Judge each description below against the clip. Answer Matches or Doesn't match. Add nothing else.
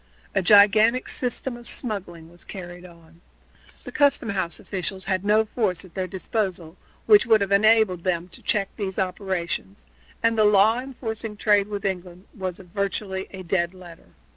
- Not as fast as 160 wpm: Doesn't match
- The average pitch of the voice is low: Doesn't match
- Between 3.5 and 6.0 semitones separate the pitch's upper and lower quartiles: Doesn't match